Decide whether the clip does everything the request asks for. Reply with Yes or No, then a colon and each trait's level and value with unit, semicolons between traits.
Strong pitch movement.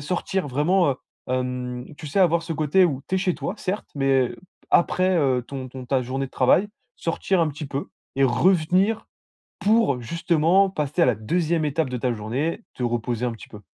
Yes: wide, 5.8 semitones